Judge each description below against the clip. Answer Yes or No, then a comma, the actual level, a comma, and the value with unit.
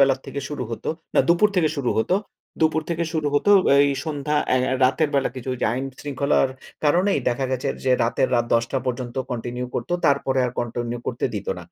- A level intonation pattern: No, average, 3.3 semitones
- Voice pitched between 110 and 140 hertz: Yes, low, 135 Hz